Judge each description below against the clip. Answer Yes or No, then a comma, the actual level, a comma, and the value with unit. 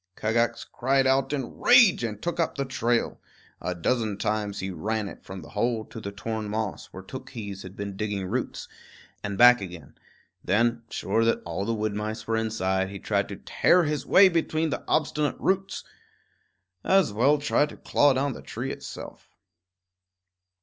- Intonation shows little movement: No, average, 5.1 semitones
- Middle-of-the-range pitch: No, low, 115 Hz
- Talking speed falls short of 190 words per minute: Yes, average, 175 wpm